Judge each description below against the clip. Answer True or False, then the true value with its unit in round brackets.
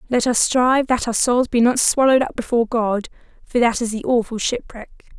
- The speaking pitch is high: True (240 Hz)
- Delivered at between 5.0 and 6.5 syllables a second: True (5.9 syllables/s)